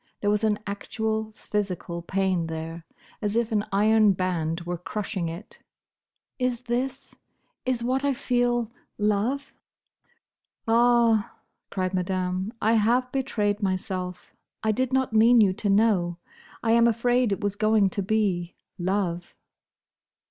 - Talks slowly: Yes, slow, 125 wpm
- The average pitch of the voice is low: No, high, 210 Hz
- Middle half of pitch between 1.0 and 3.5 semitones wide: No, average, 4.0 semitones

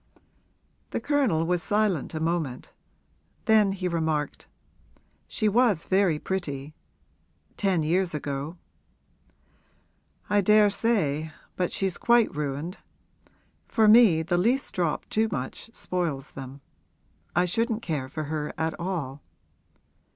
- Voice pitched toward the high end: No, medium, 175 Hz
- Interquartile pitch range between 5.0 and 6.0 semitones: Yes, average, 5.3 semitones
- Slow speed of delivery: Yes, slow, 115 wpm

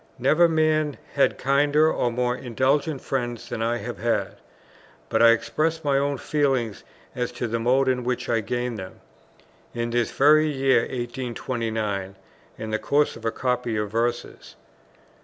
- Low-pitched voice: Yes, low, 125 Hz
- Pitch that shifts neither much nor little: Yes, average, 3.3 semitones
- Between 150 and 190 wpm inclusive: Yes, average, 160 wpm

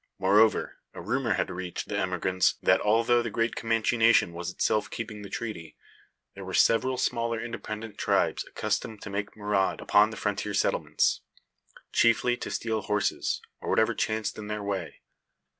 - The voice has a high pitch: No, low, 105 Hz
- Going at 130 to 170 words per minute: Yes, average, 160 wpm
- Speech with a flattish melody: Yes, narrow, 2.3 semitones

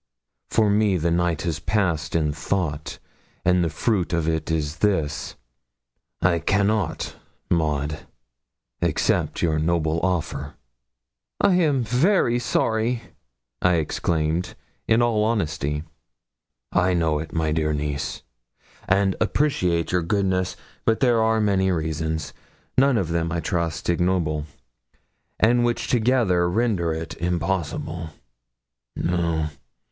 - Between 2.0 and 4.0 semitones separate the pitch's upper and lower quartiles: No, average, 4.8 semitones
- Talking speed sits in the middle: No, slow, 120 wpm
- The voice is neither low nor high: No, very low, 85 Hz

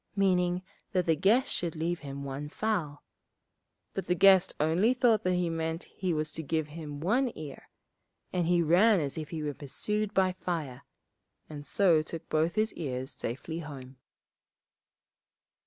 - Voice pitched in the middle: Yes, medium, 165 Hz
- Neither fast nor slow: Yes, average, 160 wpm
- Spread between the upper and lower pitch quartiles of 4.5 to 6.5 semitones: No, average, 3.7 semitones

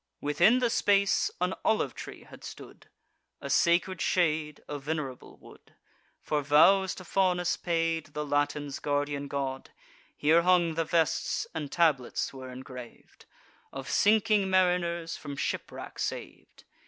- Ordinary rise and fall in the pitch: Yes, average, 3.9 semitones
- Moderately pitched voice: Yes, medium, 160 Hz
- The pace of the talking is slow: Yes, slow, 130 wpm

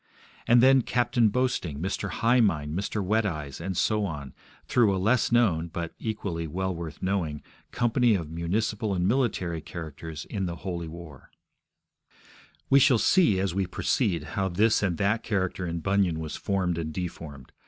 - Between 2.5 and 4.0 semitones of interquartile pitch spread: No, average, 4.7 semitones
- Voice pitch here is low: Yes, very low, 95 Hz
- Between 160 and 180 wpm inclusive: Yes, average, 165 wpm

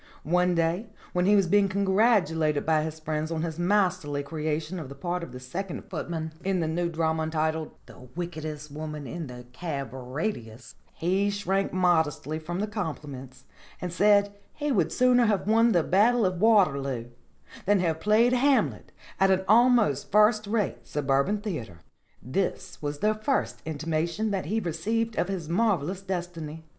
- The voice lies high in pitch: No, medium, 175 Hz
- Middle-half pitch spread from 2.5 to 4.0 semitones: No, average, 4.8 semitones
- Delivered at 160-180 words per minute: Yes, average, 165 wpm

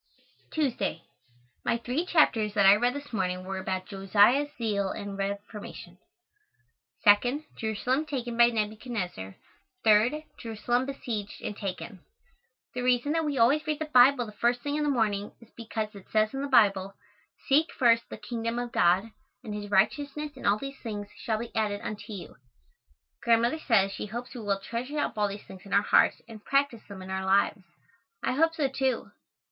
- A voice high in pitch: Yes, high, 225 Hz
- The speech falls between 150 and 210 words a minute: Yes, average, 180 wpm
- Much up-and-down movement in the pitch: No, average, 4.4 semitones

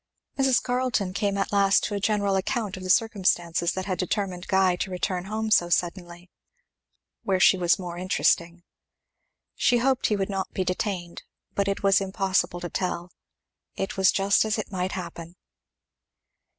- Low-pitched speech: No, high, 190 Hz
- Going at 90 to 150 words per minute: No, average, 165 wpm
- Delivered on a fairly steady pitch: Yes, narrow, 2.1 semitones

